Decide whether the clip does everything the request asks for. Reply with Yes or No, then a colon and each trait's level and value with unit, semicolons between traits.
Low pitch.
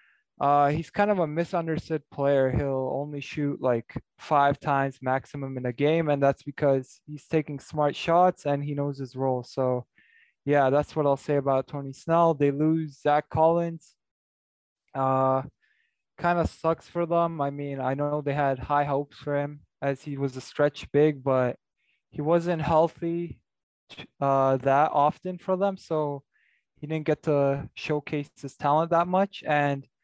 No: medium, 145 Hz